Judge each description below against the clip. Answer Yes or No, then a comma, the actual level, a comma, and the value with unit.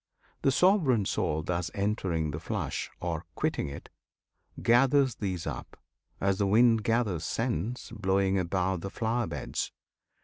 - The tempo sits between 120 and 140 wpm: Yes, slow, 135 wpm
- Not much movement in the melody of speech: No, average, 5.0 semitones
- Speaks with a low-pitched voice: Yes, low, 100 Hz